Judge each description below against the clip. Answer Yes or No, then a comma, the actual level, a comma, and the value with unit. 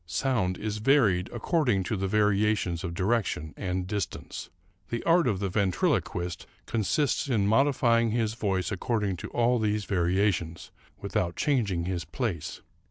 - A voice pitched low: Yes, low, 105 Hz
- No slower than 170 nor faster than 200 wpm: No, average, 140 wpm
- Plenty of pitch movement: No, average, 4.1 semitones